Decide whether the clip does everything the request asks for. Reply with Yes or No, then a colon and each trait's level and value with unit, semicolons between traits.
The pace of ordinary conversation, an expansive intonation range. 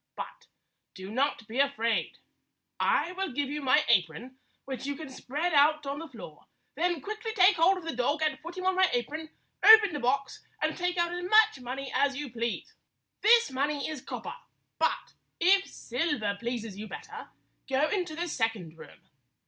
Yes: average, 180 wpm; wide, 6.0 semitones